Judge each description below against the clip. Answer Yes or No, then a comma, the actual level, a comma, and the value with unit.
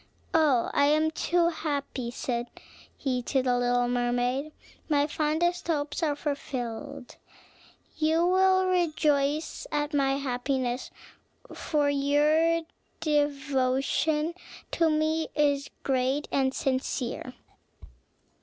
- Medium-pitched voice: No, very high, 290 Hz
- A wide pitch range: No, average, 3.1 semitones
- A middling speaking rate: No, slow, 105 wpm